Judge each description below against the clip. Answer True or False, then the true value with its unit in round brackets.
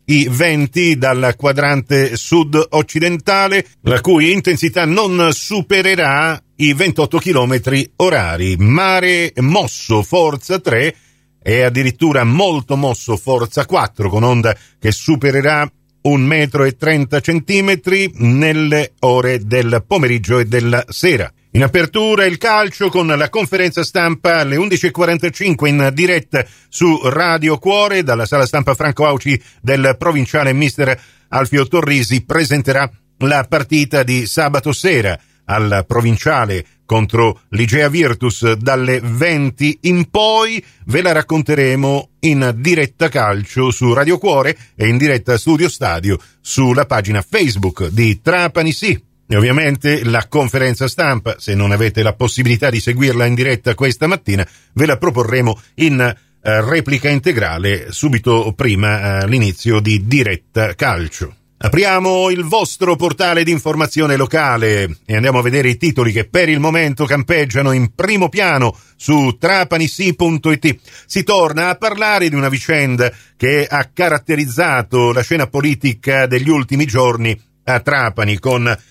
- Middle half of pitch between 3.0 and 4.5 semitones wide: False (5.2 semitones)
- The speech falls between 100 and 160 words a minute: True (130 wpm)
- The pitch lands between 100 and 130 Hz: False (140 Hz)